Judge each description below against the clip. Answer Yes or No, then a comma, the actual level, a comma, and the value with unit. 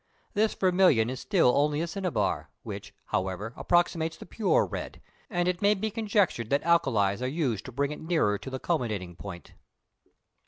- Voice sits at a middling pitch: Yes, medium, 150 Hz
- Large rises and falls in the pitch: Yes, wide, 7.8 semitones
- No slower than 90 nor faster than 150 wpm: No, average, 170 wpm